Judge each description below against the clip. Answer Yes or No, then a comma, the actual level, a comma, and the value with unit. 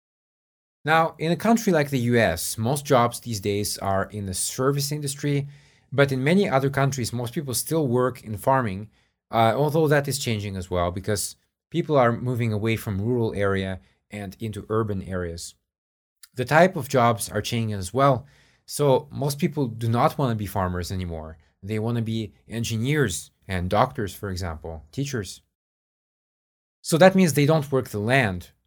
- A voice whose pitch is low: Yes, low, 115 Hz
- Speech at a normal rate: Yes, average, 170 wpm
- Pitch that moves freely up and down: Yes, wide, 6.0 semitones